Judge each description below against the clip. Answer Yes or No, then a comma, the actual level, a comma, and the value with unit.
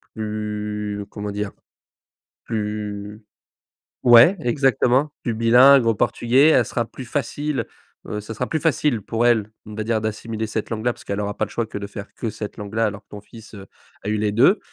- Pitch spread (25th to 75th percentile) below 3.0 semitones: Yes, narrow, 2.4 semitones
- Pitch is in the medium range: No, low, 110 Hz